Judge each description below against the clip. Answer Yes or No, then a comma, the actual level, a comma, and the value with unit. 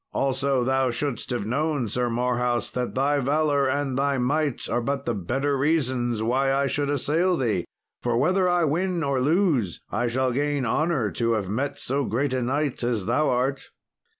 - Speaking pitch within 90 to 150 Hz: Yes, low, 135 Hz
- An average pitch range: Yes, average, 3.0 semitones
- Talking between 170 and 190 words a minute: Yes, average, 180 wpm